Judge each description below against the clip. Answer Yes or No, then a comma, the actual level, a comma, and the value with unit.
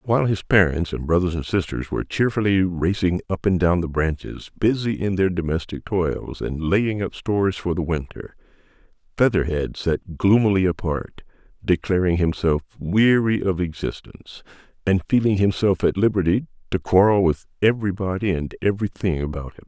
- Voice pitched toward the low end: Yes, very low, 90 Hz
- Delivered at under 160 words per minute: Yes, average, 150 wpm